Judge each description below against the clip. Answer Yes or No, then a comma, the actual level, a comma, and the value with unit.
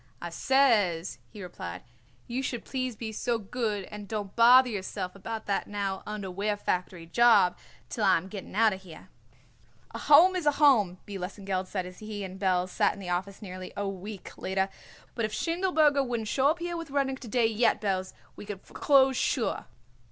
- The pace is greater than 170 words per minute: Yes, average, 190 wpm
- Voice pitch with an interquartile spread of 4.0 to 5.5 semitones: Yes, average, 4.9 semitones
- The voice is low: No, high, 210 Hz